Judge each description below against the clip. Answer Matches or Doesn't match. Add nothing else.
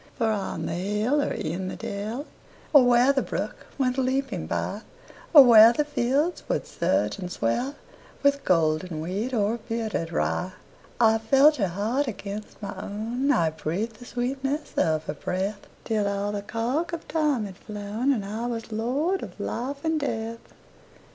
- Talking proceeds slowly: Doesn't match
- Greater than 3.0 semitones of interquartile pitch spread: Matches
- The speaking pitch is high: Matches